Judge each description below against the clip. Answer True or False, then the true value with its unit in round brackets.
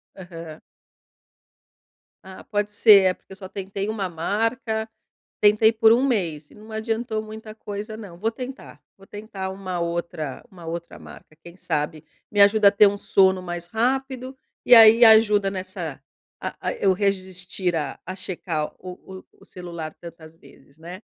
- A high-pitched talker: True (195 Hz)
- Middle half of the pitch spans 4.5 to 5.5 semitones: False (3.9 semitones)